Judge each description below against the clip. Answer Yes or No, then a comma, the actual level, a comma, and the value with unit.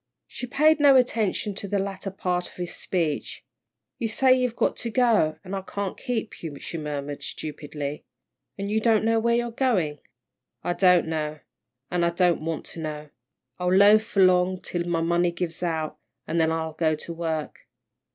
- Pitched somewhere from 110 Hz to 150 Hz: No, medium, 180 Hz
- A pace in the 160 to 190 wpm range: Yes, average, 180 wpm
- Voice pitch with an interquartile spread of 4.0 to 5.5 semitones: Yes, average, 5.1 semitones